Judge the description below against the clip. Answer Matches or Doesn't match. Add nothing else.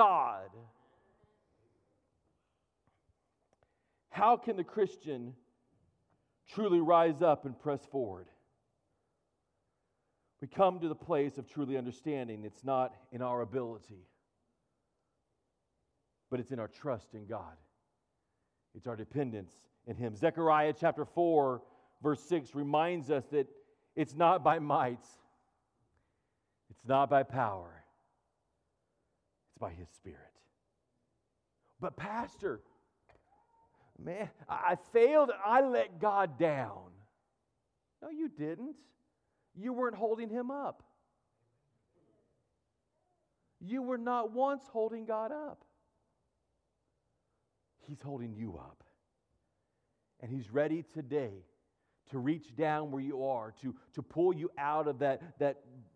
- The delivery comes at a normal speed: Doesn't match